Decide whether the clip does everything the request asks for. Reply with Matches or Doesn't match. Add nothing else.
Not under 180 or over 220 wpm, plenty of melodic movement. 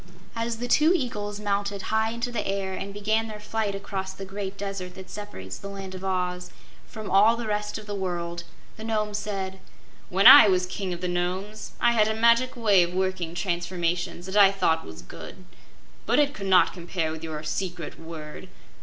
Doesn't match